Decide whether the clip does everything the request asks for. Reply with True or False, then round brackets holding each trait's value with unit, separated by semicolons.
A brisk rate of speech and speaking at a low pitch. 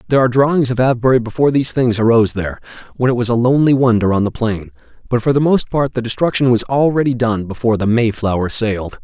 True (220 wpm; 120 Hz)